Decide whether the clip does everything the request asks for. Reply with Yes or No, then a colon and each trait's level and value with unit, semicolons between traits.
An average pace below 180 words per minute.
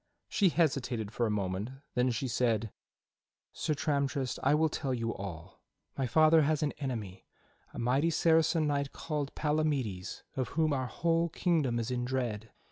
Yes: average, 160 wpm